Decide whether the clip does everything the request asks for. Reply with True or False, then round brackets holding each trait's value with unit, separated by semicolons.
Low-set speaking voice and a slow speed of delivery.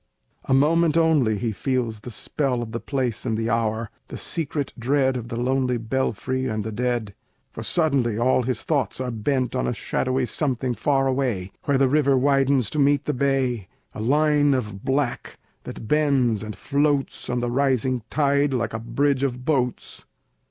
False (130 Hz; 180 wpm)